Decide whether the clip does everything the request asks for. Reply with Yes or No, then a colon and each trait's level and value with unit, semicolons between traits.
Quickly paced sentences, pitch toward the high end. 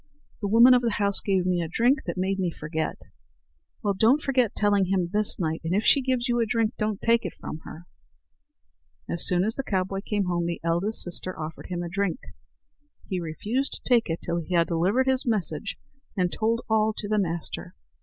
Yes: fast, 210 wpm; high, 200 Hz